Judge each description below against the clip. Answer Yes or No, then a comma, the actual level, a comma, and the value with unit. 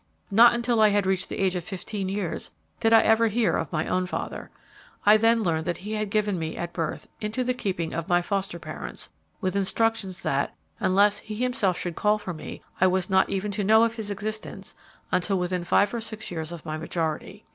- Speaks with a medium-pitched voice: No, high, 195 Hz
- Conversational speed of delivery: No, fast, 215 wpm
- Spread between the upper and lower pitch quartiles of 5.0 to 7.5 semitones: No, average, 3.6 semitones